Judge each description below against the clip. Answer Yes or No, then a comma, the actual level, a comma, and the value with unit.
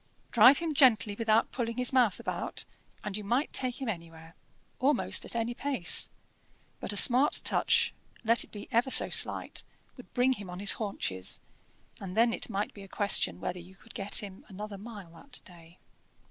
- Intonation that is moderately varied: Yes, average, 4.2 semitones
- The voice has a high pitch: Yes, high, 215 Hz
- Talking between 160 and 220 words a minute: Yes, average, 185 wpm